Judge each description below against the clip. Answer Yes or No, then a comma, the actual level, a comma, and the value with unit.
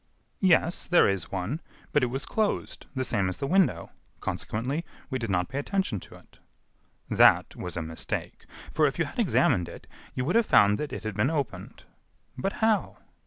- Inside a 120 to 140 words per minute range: No, average, 190 wpm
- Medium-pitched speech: No, low, 130 Hz